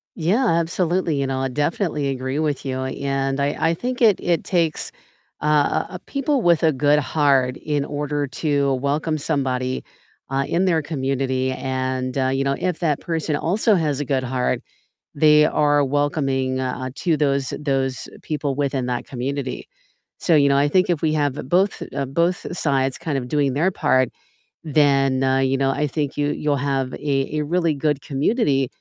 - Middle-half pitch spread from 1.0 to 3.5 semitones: Yes, average, 2.8 semitones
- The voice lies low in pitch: No, medium, 145 Hz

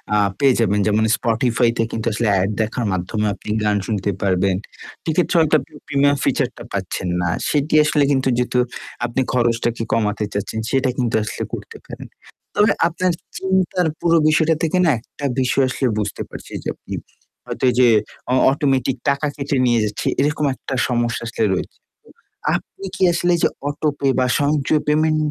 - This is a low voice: Yes, low, 130 Hz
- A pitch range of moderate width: Yes, average, 5.0 semitones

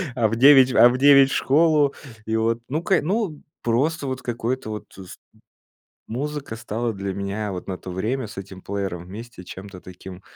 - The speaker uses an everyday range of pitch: No, wide, 5.7 semitones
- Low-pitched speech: Yes, low, 115 Hz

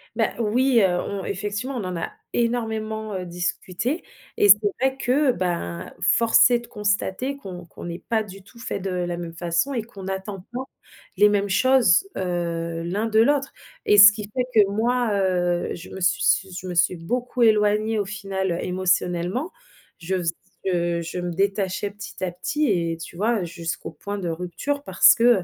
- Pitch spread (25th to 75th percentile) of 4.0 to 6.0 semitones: Yes, average, 4.4 semitones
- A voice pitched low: No, high, 200 Hz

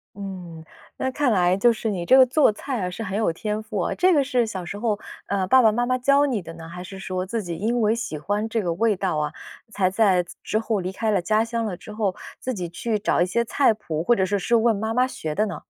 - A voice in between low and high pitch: No, high, 210 Hz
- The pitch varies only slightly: No, average, 4.0 semitones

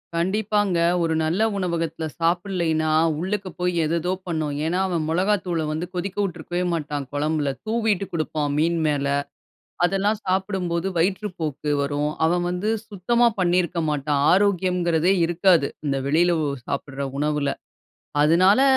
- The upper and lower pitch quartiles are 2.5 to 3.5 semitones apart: Yes, average, 3.2 semitones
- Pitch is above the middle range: No, medium, 170 Hz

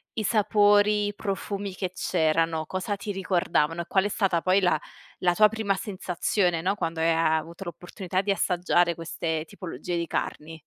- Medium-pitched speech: Yes, medium, 180 Hz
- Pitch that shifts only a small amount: No, average, 3.3 semitones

